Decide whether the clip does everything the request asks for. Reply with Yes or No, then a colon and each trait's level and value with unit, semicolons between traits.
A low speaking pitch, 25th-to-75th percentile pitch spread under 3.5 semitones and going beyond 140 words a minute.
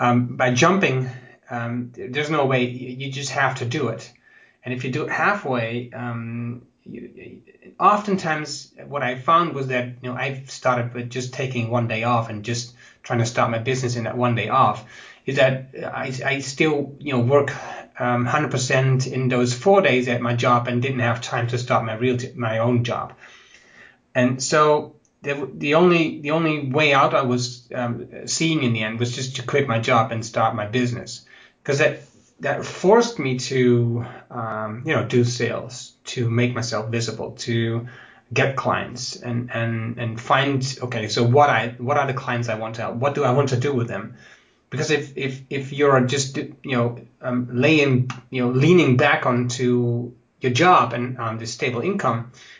Yes: low, 125 Hz; narrow, 2.4 semitones; average, 195 wpm